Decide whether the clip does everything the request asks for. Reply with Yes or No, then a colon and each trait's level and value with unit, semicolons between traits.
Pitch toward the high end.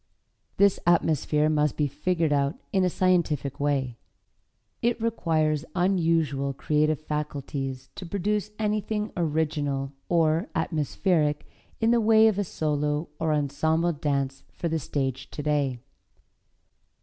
No: medium, 155 Hz